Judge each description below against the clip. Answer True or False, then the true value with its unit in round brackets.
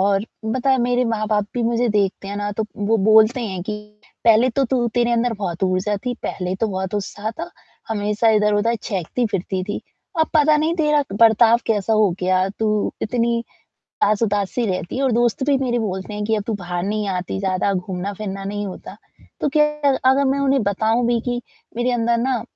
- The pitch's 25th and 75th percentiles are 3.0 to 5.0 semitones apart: True (3.3 semitones)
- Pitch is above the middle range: True (220 Hz)